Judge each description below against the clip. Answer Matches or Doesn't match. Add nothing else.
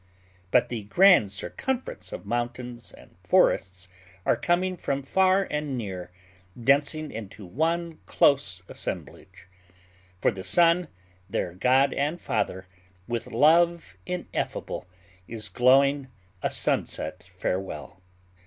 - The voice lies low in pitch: Matches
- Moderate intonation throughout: Doesn't match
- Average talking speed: Doesn't match